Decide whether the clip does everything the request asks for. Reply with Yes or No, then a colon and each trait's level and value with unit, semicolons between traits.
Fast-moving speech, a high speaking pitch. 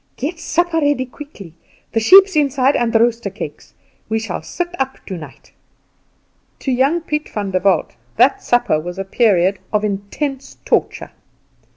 No: average, 145 wpm; high, 240 Hz